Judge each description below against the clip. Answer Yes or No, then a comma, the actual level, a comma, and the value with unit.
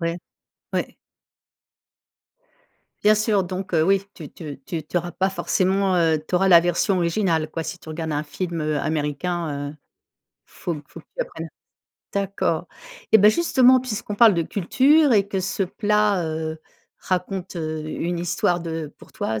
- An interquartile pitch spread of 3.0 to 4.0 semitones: Yes, average, 3.6 semitones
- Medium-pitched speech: Yes, medium, 175 Hz